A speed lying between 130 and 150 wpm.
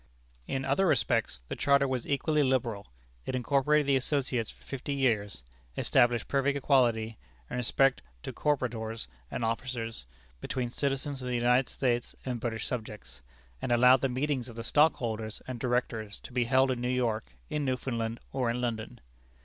No: average, 165 wpm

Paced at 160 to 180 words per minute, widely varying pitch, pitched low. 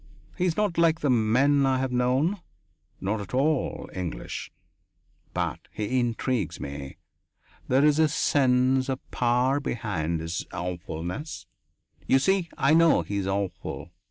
No: average, 145 wpm; wide, 6.3 semitones; low, 125 Hz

